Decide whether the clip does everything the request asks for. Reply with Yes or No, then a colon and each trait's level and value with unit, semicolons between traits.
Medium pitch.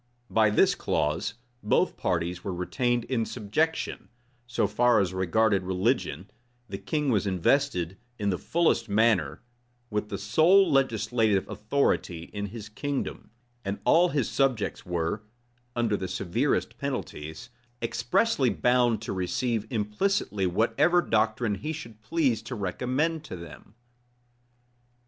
No: low, 110 Hz